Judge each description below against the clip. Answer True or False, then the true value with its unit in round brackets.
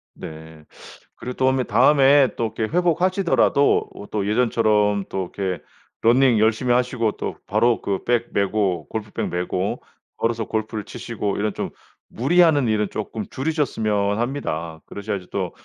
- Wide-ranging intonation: False (4.1 semitones)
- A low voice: True (110 Hz)